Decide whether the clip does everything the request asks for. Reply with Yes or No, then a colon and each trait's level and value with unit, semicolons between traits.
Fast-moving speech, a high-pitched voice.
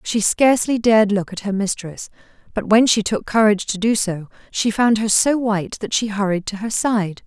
Yes: fast, 215 wpm; high, 215 Hz